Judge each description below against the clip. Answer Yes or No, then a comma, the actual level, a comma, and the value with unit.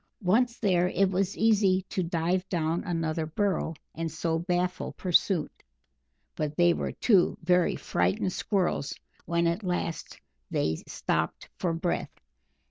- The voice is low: No, medium, 175 Hz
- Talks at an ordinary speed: No, slow, 130 wpm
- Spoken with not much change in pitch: Yes, narrow, 2.3 semitones